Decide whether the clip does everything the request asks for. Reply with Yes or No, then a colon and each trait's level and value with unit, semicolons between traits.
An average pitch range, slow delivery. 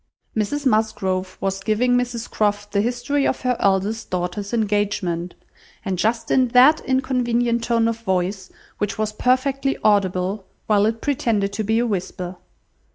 No: average, 3.8 semitones; average, 150 wpm